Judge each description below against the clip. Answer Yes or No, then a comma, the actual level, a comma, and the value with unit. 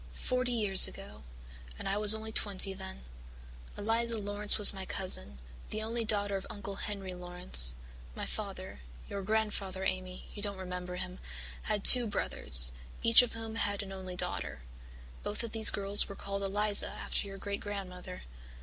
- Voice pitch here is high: Yes, high, 200 Hz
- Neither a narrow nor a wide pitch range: No, narrow, 2.3 semitones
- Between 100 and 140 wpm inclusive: No, average, 160 wpm